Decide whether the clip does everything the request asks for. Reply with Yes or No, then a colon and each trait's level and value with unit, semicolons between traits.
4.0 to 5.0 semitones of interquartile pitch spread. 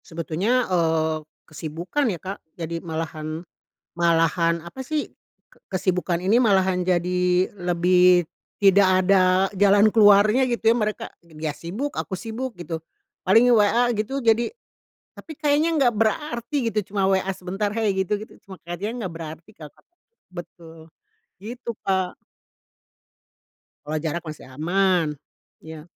Yes: average, 4.5 semitones